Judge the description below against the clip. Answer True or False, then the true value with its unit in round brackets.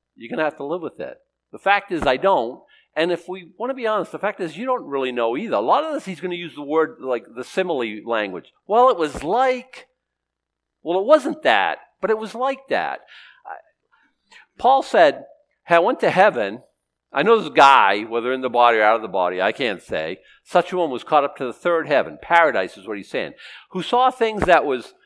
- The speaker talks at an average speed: False (230 wpm)